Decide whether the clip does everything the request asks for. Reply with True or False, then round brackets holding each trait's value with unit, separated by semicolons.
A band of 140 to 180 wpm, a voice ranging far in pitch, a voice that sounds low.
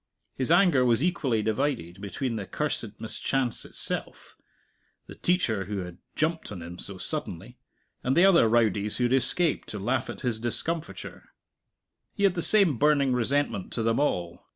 True (165 wpm; 6.3 semitones; 125 Hz)